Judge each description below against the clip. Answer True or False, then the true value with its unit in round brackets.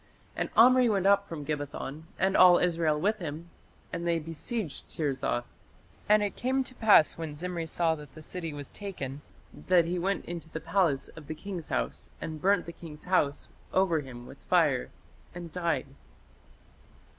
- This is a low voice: False (170 Hz)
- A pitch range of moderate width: True (4.0 semitones)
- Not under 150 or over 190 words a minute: True (170 wpm)